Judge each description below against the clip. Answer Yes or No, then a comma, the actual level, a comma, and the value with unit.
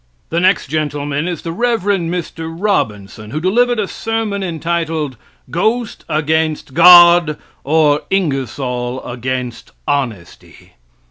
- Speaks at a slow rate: Yes, slow, 110 wpm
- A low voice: No, medium, 160 Hz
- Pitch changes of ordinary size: Yes, average, 4.7 semitones